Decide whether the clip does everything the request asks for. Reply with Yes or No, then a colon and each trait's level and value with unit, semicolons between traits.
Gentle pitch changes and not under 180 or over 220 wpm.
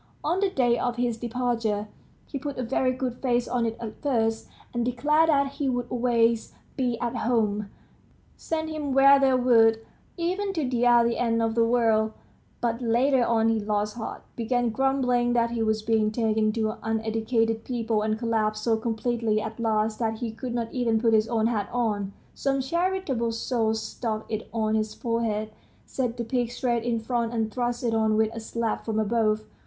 Yes: narrow, 1.9 semitones; average, 190 wpm